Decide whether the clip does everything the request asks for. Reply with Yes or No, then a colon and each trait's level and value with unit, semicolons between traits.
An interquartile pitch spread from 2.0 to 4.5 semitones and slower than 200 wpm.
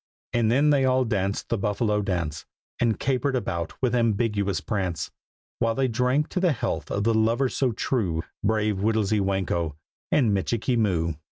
Yes: average, 4.1 semitones; average, 165 wpm